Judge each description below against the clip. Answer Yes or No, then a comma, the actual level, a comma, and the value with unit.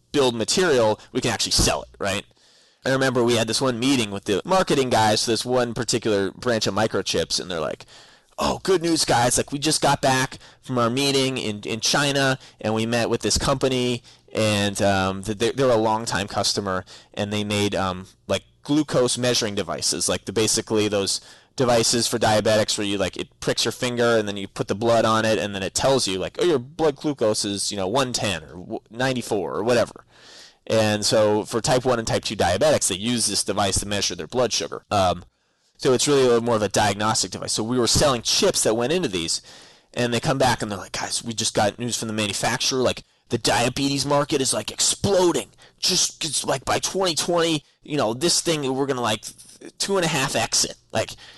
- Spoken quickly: Yes, fast, 215 wpm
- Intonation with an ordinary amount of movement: Yes, average, 4.0 semitones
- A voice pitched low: Yes, low, 115 Hz